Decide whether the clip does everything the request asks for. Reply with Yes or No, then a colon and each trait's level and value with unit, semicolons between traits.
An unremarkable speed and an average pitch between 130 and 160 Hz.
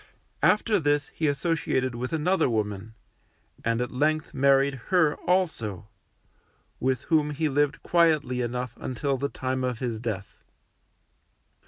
No: slow, 130 wpm; low, 135 Hz